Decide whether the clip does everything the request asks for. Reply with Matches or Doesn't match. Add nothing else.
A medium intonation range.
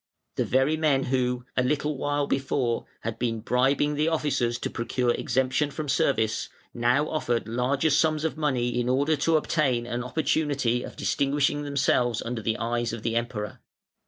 Matches